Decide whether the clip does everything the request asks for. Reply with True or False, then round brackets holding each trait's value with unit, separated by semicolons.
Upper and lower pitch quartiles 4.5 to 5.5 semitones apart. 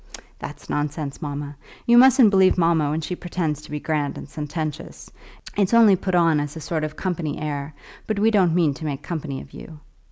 False (3.7 semitones)